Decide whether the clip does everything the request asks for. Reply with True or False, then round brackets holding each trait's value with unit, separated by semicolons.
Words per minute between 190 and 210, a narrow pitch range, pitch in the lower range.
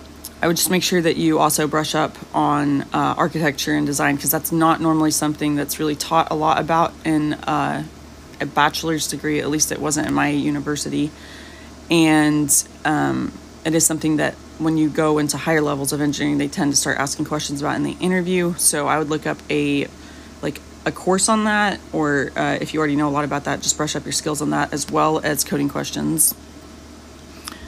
False (205 wpm; 1.8 semitones; 150 Hz)